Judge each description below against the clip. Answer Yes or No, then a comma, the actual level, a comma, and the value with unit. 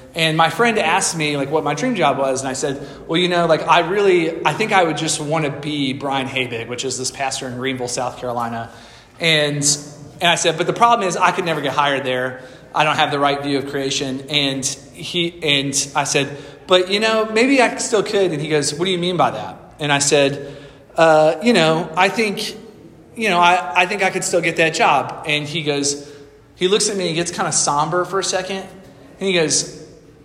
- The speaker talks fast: Yes, fast, 235 wpm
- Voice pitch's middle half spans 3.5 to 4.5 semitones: Yes, average, 4.2 semitones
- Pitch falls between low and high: Yes, medium, 155 Hz